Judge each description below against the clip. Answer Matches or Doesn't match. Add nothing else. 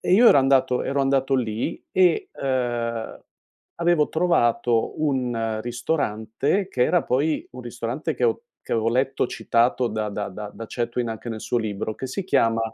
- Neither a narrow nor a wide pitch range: Matches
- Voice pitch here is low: Matches